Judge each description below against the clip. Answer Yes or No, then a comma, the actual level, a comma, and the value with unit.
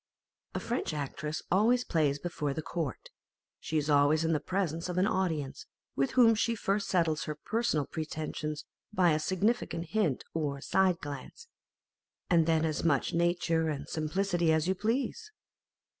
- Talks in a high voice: No, medium, 165 Hz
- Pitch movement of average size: Yes, average, 3.9 semitones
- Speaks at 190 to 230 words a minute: No, average, 160 wpm